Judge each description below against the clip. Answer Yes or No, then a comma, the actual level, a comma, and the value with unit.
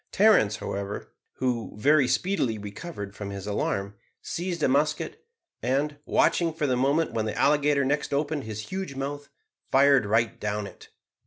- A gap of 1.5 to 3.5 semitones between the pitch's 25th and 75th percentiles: No, wide, 5.6 semitones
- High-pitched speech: No, low, 135 Hz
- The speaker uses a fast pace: No, average, 155 wpm